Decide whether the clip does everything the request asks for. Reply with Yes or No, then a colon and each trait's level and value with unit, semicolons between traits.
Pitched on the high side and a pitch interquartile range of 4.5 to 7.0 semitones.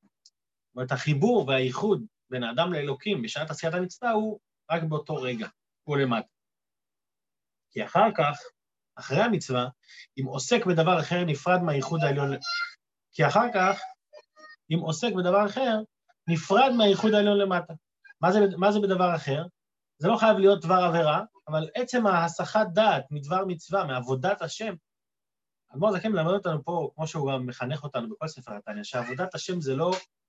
No: medium, 180 Hz; wide, 5.6 semitones